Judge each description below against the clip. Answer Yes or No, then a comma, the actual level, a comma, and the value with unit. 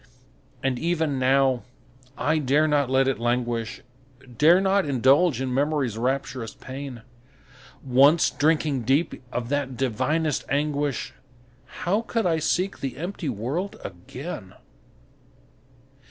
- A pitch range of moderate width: Yes, average, 3.7 semitones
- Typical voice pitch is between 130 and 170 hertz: Yes, medium, 140 Hz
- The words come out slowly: Yes, slow, 115 wpm